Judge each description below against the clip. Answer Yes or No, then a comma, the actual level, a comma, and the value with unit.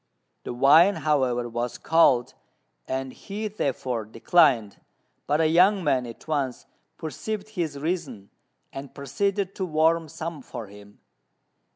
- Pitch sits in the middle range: Yes, medium, 145 Hz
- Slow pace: Yes, slow, 130 wpm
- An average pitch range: No, wide, 5.7 semitones